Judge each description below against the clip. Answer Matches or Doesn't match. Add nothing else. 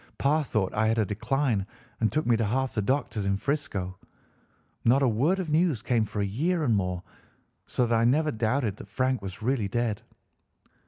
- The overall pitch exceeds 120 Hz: Doesn't match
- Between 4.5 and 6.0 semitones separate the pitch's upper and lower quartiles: Matches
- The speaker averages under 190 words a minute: Doesn't match